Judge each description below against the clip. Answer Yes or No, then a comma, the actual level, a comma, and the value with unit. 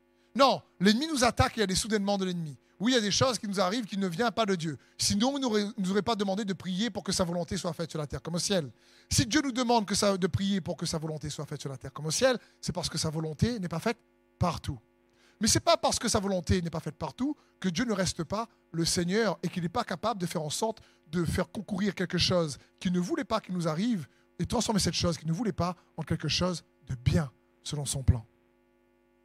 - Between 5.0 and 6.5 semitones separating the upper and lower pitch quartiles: Yes, average, 5.3 semitones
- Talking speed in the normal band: No, fast, 270 wpm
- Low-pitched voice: No, medium, 180 Hz